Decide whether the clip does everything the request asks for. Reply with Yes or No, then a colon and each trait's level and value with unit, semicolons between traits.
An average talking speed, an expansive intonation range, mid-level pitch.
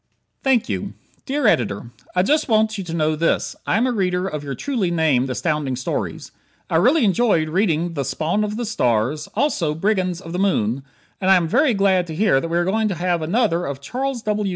No: fast, 215 wpm; wide, 5.7 semitones; medium, 180 Hz